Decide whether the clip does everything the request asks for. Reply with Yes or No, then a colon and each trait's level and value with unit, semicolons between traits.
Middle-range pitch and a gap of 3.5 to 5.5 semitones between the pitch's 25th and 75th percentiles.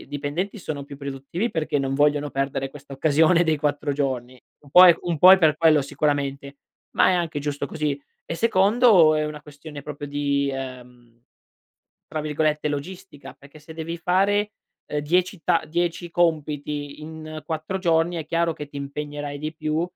No: medium, 150 Hz; average, 2.7 semitones